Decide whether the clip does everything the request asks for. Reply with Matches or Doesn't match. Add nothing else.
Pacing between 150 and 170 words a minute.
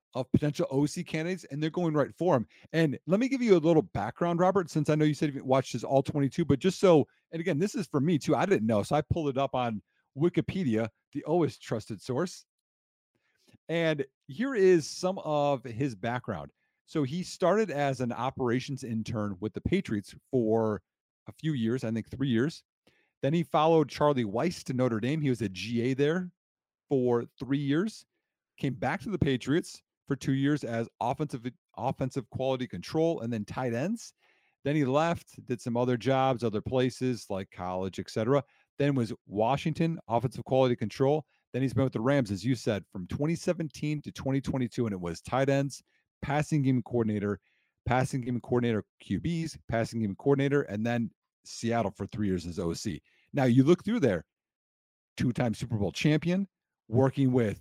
Doesn't match